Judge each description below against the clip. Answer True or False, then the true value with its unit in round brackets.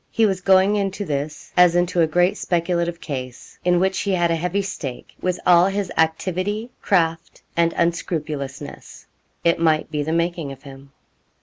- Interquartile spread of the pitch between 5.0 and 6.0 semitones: False (2.8 semitones)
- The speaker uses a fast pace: False (170 wpm)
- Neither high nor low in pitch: True (170 Hz)